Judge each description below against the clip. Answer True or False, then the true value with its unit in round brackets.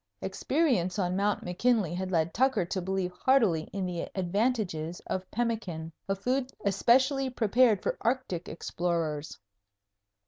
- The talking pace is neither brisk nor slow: False (130 wpm)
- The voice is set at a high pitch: True (195 Hz)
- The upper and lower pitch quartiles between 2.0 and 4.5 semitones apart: False (5.5 semitones)